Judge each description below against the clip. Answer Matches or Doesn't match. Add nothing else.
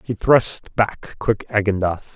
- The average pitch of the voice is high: Doesn't match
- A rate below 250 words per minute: Matches